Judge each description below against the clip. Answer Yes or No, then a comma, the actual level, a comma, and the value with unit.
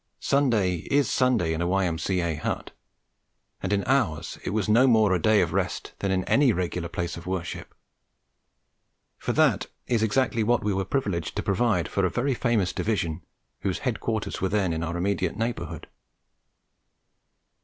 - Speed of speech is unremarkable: Yes, average, 170 wpm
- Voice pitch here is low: Yes, low, 100 Hz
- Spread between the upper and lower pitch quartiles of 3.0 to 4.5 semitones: No, average, 4.9 semitones